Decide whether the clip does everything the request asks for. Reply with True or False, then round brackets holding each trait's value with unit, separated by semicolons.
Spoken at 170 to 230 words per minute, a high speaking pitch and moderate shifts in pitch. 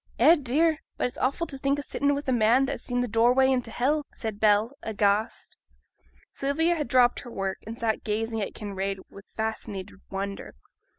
True (190 wpm; 240 Hz; 4.4 semitones)